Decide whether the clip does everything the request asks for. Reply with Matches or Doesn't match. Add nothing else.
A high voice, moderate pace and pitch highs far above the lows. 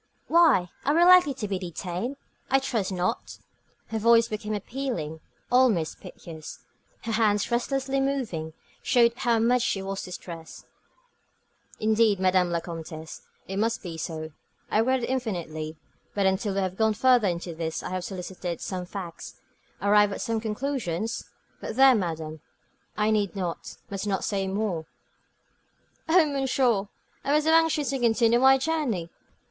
Matches